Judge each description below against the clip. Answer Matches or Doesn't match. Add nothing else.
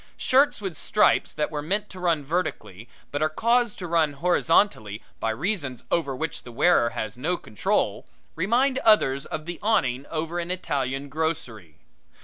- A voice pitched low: Doesn't match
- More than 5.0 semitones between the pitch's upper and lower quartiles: Matches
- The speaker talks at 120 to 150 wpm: Doesn't match